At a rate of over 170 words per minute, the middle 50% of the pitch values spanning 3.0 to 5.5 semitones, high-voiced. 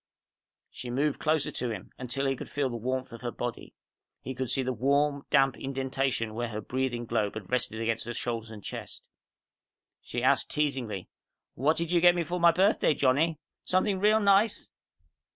No: average, 185 wpm; average, 4.3 semitones; low, 130 Hz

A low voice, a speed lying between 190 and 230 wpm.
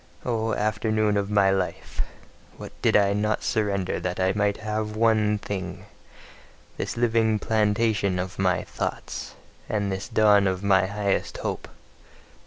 No: low, 105 Hz; average, 140 wpm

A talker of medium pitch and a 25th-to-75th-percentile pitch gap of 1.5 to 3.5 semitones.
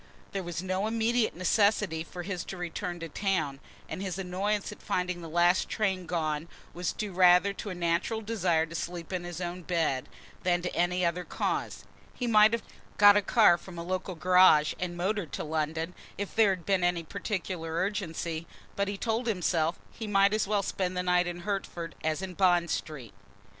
Yes: medium, 180 Hz; average, 2.7 semitones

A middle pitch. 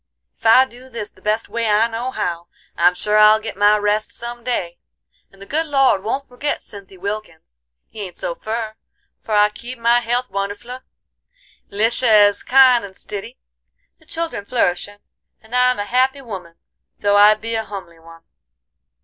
No: high, 215 Hz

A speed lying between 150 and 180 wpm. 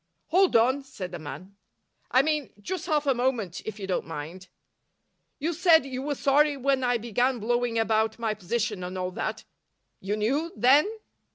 Yes: average, 175 wpm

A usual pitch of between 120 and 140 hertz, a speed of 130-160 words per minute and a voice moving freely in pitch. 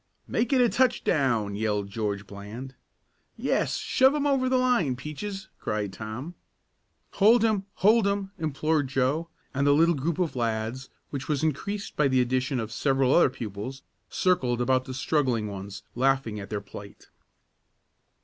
Yes: low, 135 Hz; average, 155 wpm; wide, 8.1 semitones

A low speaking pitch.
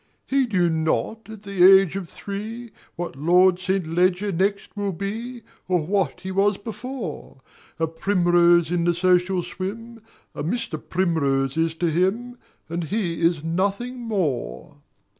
No: medium, 185 Hz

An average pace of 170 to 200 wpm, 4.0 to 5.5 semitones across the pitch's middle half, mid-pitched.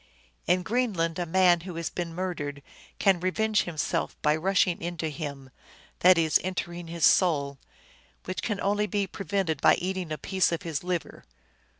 No: average, 175 wpm; average, 2.8 semitones; medium, 175 Hz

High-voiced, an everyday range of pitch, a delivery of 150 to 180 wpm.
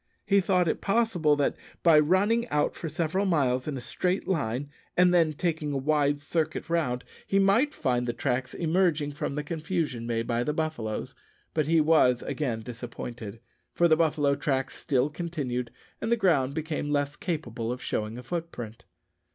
No: medium, 150 Hz; average, 5.0 semitones; average, 175 wpm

